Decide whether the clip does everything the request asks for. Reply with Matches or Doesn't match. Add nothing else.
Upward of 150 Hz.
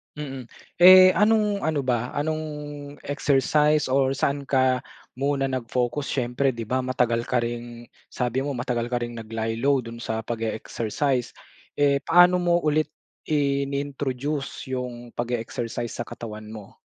Doesn't match